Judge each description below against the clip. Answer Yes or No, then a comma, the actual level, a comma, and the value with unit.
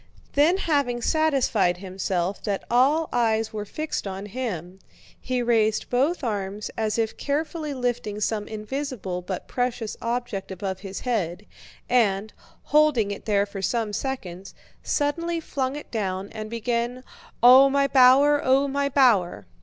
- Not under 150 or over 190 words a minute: No, average, 140 wpm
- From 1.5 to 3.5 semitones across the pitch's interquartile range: No, average, 5.2 semitones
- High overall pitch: Yes, high, 235 Hz